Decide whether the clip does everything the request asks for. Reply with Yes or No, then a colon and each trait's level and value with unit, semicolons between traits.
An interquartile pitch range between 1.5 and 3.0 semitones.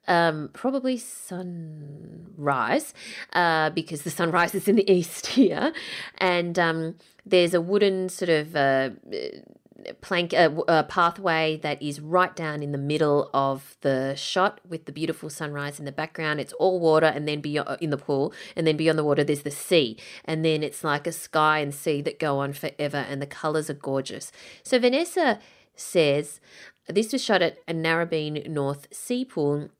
No: average, 3.4 semitones